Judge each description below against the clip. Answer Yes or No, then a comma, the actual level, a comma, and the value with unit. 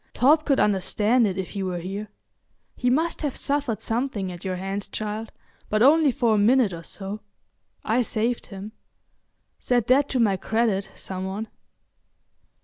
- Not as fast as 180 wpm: Yes, average, 160 wpm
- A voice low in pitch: No, high, 215 Hz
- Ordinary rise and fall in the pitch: Yes, average, 4.4 semitones